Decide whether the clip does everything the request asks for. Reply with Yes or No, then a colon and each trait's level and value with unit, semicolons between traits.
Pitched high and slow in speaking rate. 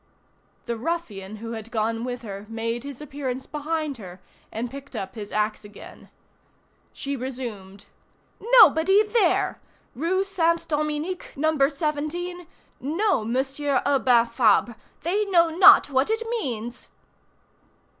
Yes: very high, 275 Hz; slow, 125 wpm